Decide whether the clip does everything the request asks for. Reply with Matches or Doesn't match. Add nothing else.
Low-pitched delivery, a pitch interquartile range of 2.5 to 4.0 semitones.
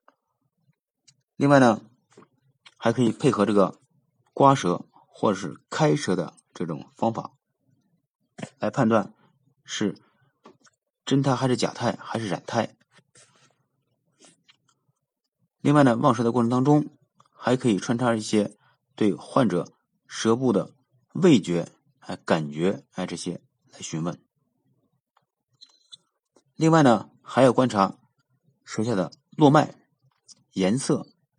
Matches